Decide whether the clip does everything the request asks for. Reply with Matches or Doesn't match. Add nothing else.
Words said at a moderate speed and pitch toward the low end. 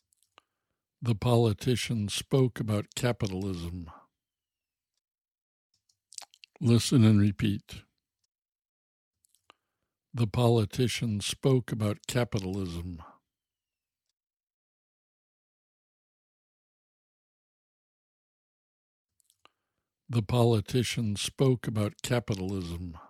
Doesn't match